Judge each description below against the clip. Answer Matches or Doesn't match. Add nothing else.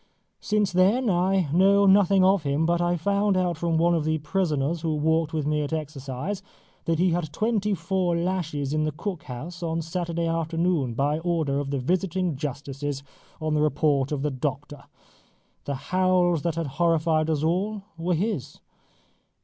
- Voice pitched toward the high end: Doesn't match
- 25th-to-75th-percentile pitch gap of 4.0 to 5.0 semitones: Doesn't match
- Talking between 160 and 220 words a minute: Matches